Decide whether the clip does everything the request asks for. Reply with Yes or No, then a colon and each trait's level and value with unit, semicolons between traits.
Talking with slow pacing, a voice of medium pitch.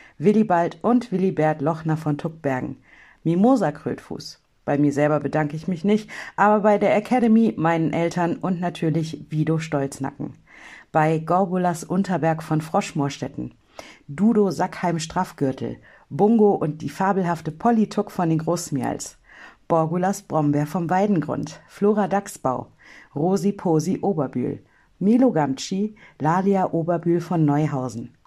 Yes: slow, 120 wpm; medium, 170 Hz